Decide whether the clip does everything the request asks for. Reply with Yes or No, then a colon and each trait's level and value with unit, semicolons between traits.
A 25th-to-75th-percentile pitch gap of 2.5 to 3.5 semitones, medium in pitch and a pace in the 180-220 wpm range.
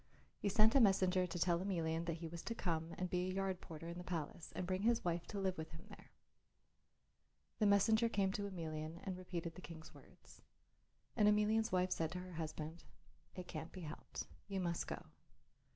Yes: average, 2.8 semitones; medium, 180 Hz; average, 200 wpm